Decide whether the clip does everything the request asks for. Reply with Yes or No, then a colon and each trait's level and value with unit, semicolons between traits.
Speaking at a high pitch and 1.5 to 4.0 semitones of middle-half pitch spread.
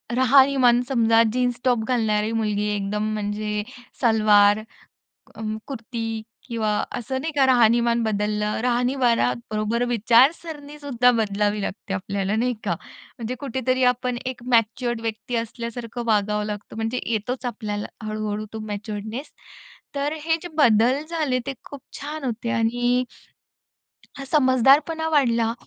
Yes: high, 235 Hz; average, 3.2 semitones